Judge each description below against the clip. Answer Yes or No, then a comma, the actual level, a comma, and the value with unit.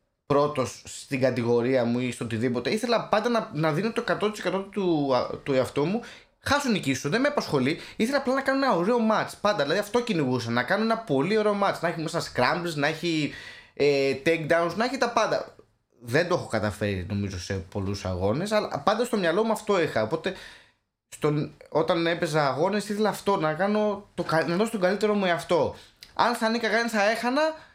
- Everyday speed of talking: No, fast, 195 wpm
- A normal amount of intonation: No, wide, 7.8 semitones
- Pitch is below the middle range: No, medium, 175 Hz